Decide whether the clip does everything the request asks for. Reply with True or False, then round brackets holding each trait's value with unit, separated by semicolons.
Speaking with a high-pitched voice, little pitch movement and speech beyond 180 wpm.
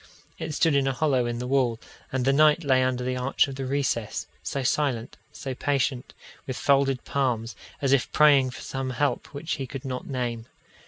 False (135 Hz; 1.9 semitones; 200 wpm)